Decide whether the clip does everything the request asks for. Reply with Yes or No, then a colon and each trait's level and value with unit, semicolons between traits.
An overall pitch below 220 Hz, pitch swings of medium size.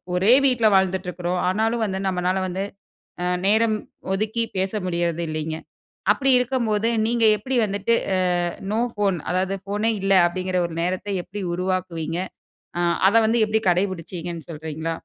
Yes: high, 190 Hz; average, 3.5 semitones